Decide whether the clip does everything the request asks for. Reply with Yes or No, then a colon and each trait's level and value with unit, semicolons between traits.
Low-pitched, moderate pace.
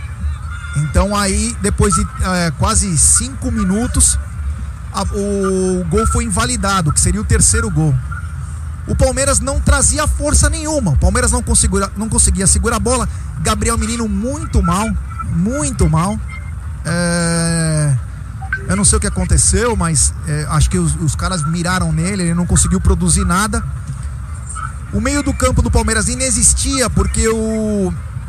Yes: low, 110 Hz; average, 150 wpm